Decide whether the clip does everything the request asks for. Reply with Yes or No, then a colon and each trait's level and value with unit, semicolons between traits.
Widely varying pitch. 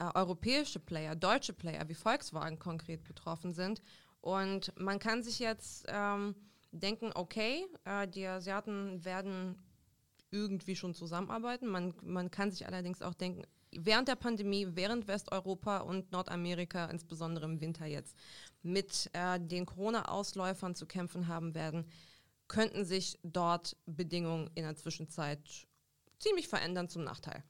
No: average, 2.9 semitones